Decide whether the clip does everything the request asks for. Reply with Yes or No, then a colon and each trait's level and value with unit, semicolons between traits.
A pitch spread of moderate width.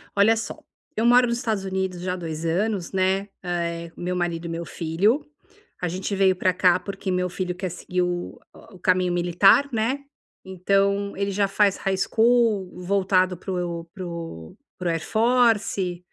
No: narrow, 2.2 semitones